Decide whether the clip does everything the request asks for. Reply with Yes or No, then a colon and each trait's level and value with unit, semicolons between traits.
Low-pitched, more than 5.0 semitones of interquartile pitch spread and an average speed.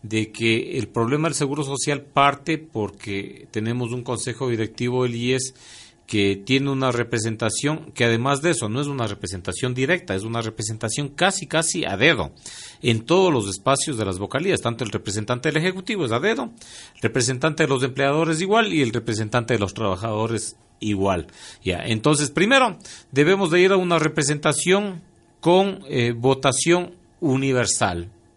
Yes: low, 130 Hz; wide, 5.5 semitones; average, 160 wpm